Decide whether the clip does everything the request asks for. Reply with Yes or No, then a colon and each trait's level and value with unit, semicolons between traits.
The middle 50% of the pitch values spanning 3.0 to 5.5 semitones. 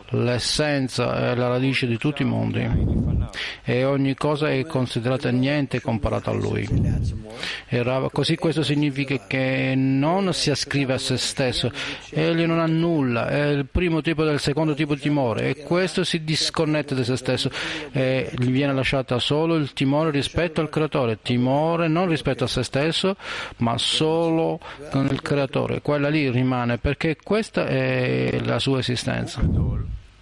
Yes: average, 3.6 semitones